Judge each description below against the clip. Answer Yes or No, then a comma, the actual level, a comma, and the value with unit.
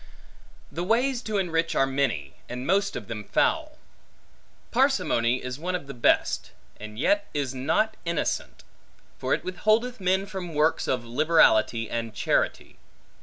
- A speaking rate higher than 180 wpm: No, average, 145 wpm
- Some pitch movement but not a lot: No, wide, 7.6 semitones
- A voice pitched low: No, medium, 160 Hz